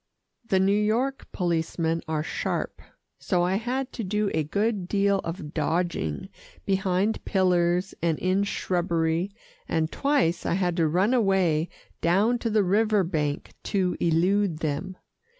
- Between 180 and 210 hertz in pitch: Yes, medium, 185 Hz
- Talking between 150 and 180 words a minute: No, average, 140 wpm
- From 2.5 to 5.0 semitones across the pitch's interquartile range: Yes, average, 3.5 semitones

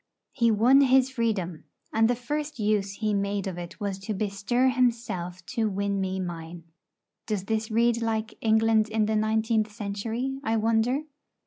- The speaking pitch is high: Yes, high, 220 Hz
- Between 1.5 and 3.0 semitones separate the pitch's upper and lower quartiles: Yes, average, 2.7 semitones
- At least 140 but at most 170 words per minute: Yes, average, 160 wpm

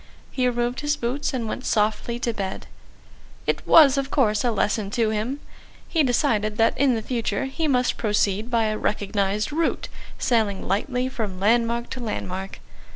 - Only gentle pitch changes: No, average, 3.4 semitones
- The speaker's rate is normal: Yes, average, 165 wpm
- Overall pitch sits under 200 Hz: No, high, 235 Hz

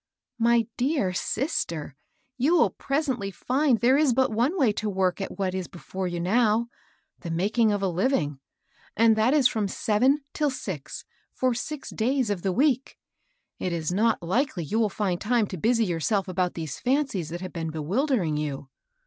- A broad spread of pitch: Yes, wide, 6.0 semitones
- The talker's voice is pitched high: Yes, high, 215 Hz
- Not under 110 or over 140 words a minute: No, average, 190 wpm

